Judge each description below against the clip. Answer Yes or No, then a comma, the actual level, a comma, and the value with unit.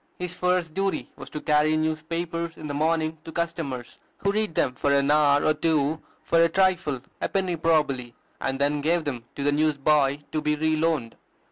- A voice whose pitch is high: No, medium, 155 Hz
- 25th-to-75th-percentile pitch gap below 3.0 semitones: Yes, narrow, 2.6 semitones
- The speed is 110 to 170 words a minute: No, average, 195 wpm